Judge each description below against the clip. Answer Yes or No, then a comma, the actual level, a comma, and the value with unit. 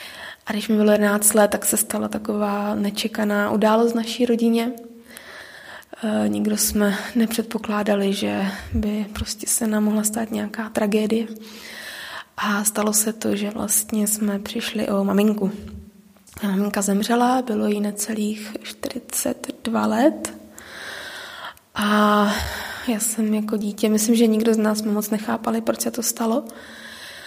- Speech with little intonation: Yes, narrow, 1.7 semitones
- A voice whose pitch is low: No, high, 215 Hz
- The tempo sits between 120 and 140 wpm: Yes, average, 135 wpm